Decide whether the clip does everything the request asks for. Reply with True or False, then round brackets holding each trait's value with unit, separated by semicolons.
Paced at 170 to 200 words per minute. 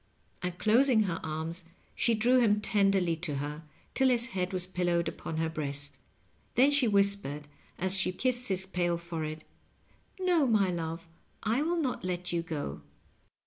False (160 wpm)